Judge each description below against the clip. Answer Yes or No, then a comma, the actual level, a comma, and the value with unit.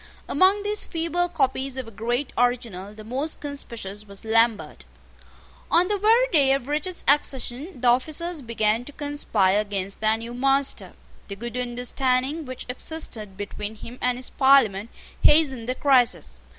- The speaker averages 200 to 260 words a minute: No, average, 150 wpm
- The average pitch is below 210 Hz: No, very high, 250 Hz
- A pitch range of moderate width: Yes, average, 4.7 semitones